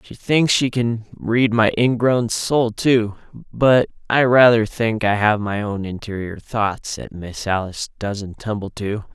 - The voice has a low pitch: Yes, low, 110 Hz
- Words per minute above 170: No, average, 155 wpm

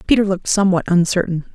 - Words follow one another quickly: No, average, 155 wpm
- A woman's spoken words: Yes, female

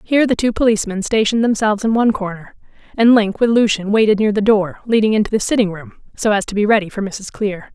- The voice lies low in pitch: No, high, 215 Hz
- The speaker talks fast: Yes, fast, 230 wpm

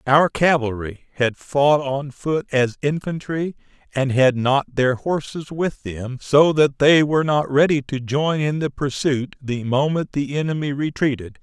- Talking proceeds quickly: No, average, 165 wpm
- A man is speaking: Yes, male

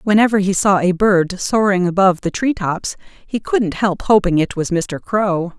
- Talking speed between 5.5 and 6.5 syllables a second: No, 4.6 syllables/s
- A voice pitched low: No, high, 190 Hz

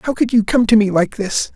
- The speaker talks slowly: No, fast, 310 wpm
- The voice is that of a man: Yes, male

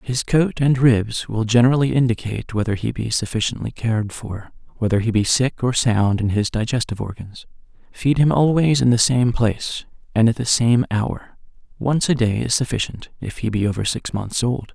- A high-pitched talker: No, low, 120 Hz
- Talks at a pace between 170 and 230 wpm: Yes, average, 190 wpm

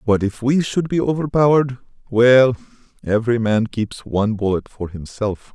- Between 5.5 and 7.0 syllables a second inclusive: No, 5.0 syllables/s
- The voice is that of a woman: No, male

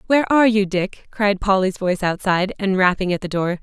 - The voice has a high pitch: Yes, high, 195 Hz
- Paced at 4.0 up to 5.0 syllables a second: No, 6.0 syllables/s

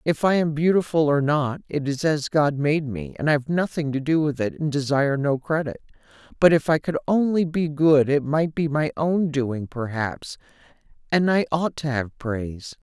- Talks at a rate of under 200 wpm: No, fast, 205 wpm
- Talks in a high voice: No, medium, 150 Hz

